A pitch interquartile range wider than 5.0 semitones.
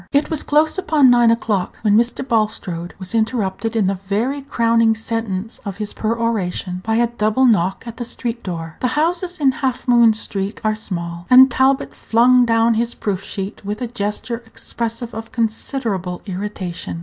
No: average, 3.4 semitones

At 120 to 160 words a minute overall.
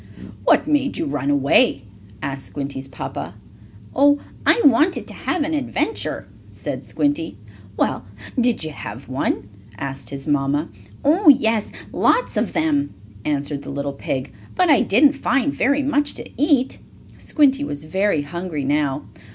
Yes: average, 145 wpm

